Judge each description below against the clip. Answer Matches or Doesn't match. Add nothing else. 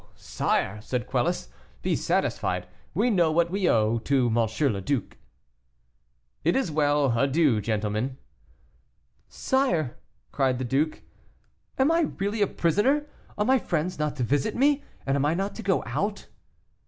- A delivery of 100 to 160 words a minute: Matches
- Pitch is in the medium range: Matches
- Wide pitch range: Matches